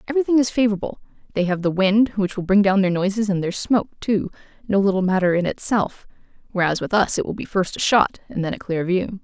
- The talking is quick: Yes, fast, 235 wpm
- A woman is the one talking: Yes, female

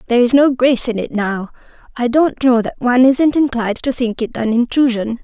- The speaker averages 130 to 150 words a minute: No, fast, 205 wpm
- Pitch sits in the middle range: No, high, 245 Hz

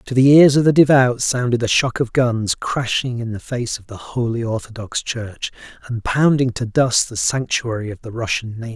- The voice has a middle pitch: No, low, 120 Hz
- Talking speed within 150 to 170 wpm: No, fast, 205 wpm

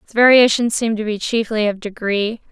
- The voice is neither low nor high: No, high, 220 Hz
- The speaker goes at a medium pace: Yes, average, 190 wpm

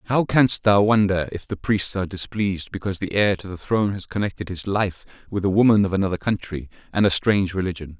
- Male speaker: Yes, male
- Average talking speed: No, fast, 220 wpm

